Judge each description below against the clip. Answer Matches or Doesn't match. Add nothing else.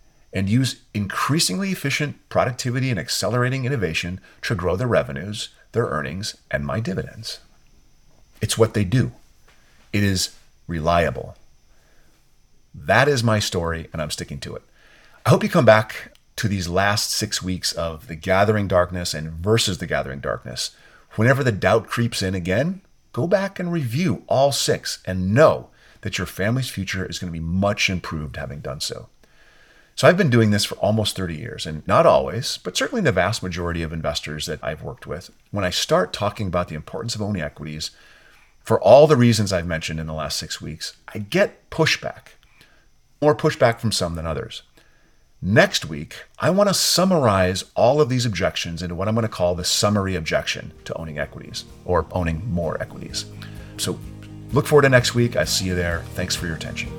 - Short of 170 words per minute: Doesn't match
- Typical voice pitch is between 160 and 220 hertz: Doesn't match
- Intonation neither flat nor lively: Doesn't match